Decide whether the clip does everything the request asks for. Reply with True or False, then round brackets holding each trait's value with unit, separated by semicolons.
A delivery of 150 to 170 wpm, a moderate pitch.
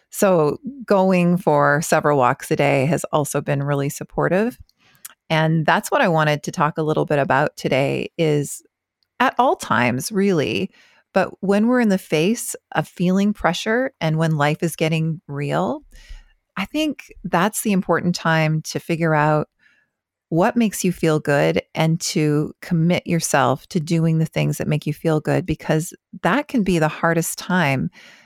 True (165 wpm; 165 Hz)